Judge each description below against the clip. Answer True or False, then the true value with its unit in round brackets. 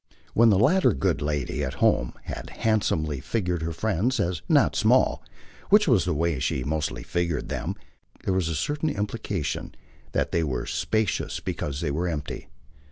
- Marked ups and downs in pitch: True (6.7 semitones)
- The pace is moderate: True (165 wpm)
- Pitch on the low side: True (85 Hz)